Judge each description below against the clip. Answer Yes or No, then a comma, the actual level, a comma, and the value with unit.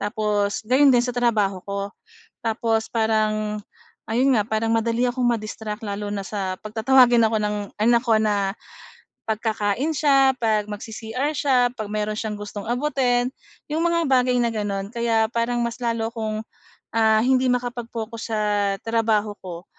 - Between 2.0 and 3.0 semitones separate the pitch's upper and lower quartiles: Yes, narrow, 2.5 semitones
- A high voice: Yes, high, 225 Hz